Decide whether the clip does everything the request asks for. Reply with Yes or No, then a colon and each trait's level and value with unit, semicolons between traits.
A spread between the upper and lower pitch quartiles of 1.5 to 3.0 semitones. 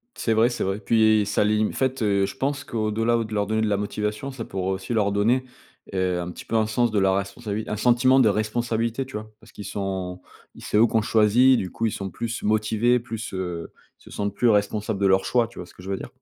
Yes: narrow, 2.6 semitones